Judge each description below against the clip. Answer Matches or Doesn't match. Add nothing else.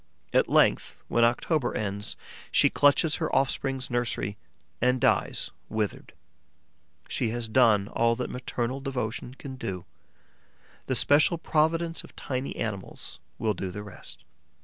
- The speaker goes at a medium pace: Doesn't match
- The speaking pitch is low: Matches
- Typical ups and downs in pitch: Matches